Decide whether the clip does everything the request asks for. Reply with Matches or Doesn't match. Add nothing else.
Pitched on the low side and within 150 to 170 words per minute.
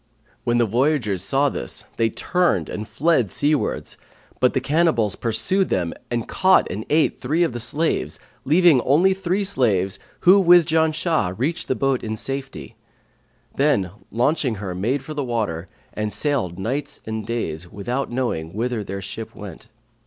Matches